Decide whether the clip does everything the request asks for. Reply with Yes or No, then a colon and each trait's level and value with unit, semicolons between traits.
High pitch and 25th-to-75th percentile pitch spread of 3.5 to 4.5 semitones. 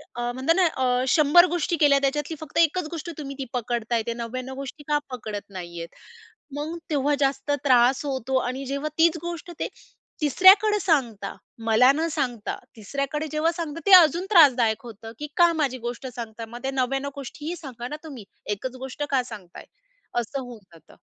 Yes: very high, 270 Hz; average, 4.2 semitones